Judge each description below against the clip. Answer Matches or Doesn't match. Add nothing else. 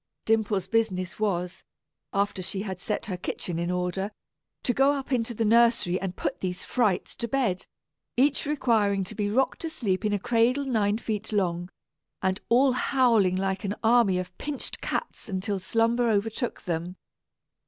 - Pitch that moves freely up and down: Doesn't match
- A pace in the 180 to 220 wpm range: Doesn't match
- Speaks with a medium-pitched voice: Doesn't match